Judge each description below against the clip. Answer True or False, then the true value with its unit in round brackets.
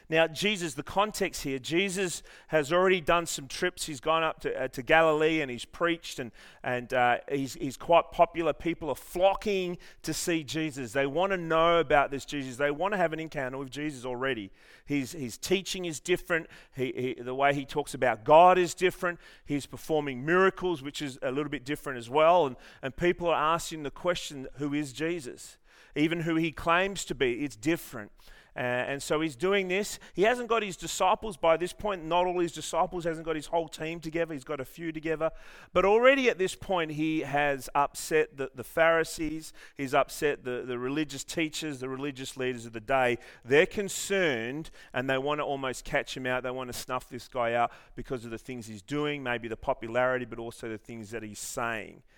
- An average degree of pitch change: True (4.5 semitones)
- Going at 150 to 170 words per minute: False (205 wpm)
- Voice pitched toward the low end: False (155 Hz)